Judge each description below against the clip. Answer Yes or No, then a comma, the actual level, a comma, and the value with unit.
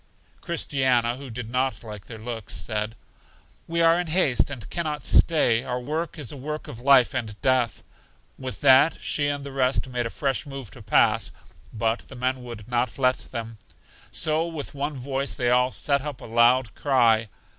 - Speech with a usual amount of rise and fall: Yes, average, 3.3 semitones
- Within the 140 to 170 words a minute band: No, average, 190 wpm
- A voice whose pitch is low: Yes, low, 130 Hz